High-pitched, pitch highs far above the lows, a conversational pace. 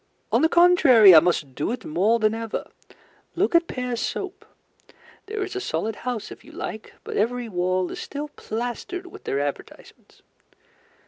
Yes: high, 235 Hz; wide, 8.6 semitones; average, 170 wpm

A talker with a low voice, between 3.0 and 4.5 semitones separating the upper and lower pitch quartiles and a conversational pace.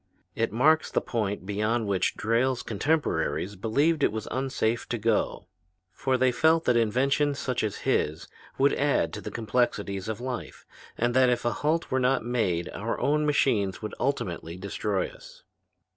Yes: low, 120 Hz; average, 4.1 semitones; average, 165 wpm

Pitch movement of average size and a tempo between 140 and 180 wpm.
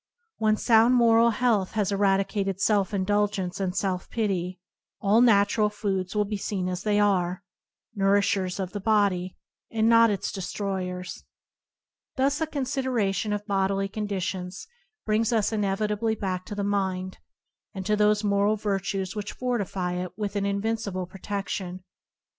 No: narrow, 2.1 semitones; average, 145 wpm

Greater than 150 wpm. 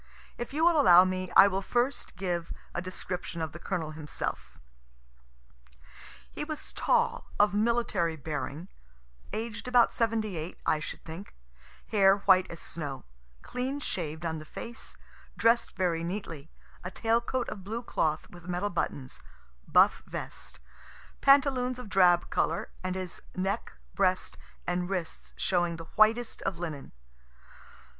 No: average, 140 wpm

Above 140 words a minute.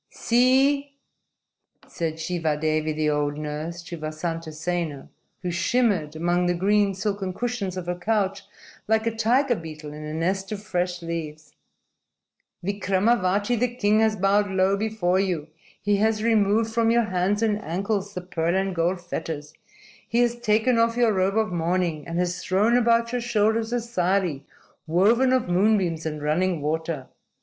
Yes: average, 160 wpm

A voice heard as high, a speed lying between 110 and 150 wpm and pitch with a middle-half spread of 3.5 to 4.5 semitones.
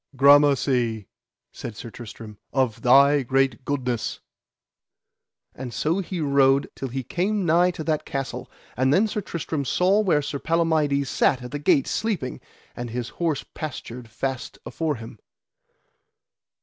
No: medium, 140 Hz; average, 140 wpm; average, 4.2 semitones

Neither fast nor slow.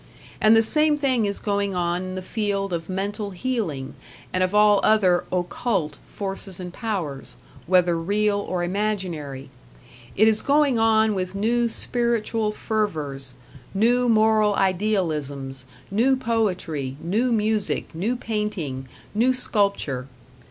No: slow, 130 wpm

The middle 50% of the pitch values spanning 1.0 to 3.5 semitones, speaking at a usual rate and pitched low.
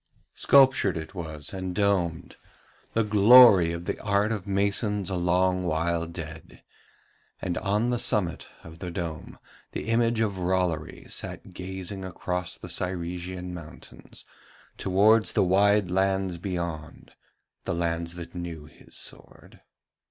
No: average, 2.9 semitones; slow, 130 wpm; very low, 90 Hz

